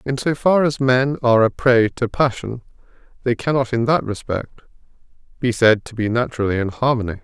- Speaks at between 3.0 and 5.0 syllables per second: No, 5.6 syllables/s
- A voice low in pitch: Yes, low, 120 Hz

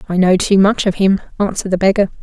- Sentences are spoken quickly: Yes, fast, 240 wpm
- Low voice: No, high, 195 Hz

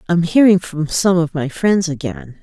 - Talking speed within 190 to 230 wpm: Yes, average, 200 wpm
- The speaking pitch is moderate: Yes, medium, 165 Hz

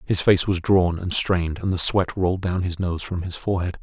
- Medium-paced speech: No, fast, 250 wpm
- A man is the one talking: Yes, male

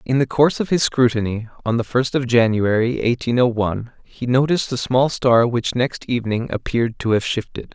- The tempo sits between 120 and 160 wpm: No, average, 200 wpm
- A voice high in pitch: No, low, 120 Hz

